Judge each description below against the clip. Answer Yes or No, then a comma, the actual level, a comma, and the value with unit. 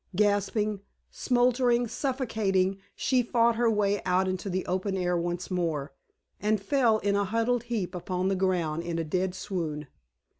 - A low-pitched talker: No, high, 195 Hz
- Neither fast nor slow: Yes, average, 155 wpm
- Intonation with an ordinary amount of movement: Yes, average, 3.9 semitones